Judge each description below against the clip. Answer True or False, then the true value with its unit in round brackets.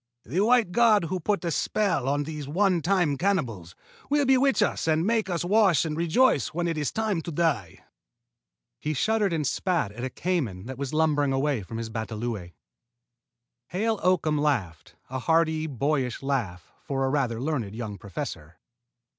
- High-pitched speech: False (155 Hz)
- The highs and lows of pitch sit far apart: True (6.6 semitones)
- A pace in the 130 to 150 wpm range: False (170 wpm)